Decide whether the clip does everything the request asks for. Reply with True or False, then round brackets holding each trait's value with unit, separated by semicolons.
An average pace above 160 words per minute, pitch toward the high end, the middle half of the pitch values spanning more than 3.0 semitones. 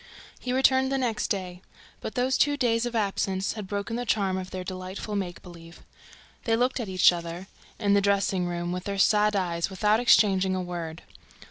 True (195 wpm; 195 Hz; 3.8 semitones)